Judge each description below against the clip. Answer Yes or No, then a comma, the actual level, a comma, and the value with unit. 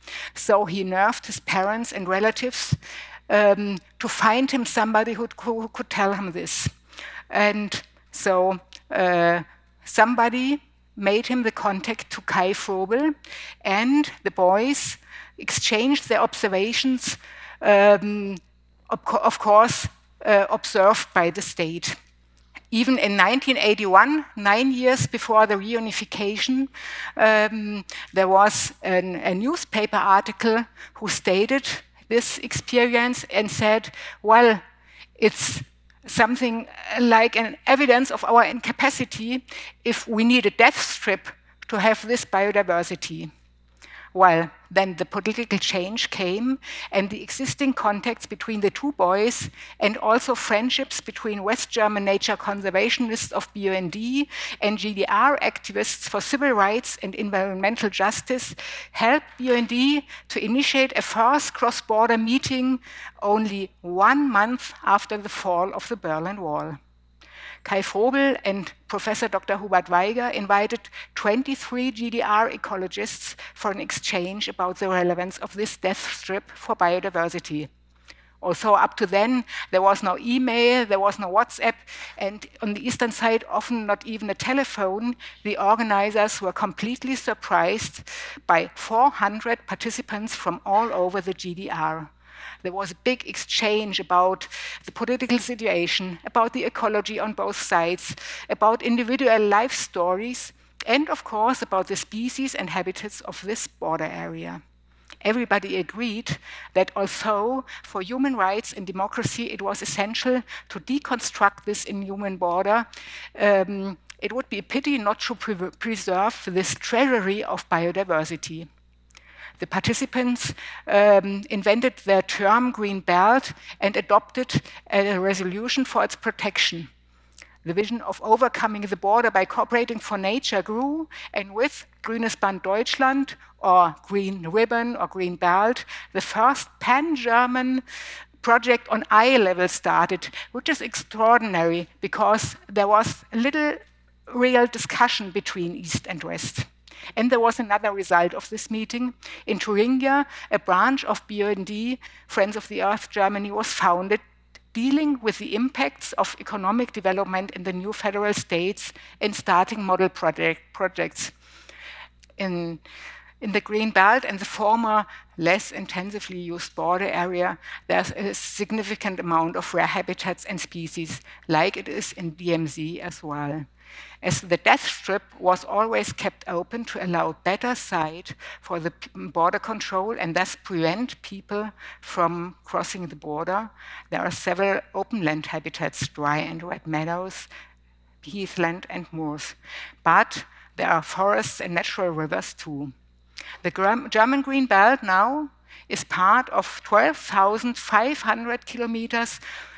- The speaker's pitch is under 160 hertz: No, high, 205 Hz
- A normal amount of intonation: Yes, average, 4.1 semitones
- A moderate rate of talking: No, slow, 130 wpm